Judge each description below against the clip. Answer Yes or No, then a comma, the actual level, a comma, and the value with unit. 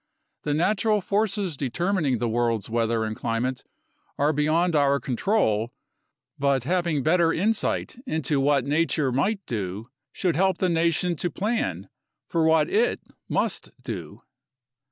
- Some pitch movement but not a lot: No, wide, 6.4 semitones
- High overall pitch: No, medium, 150 Hz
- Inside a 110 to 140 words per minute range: Yes, slow, 135 wpm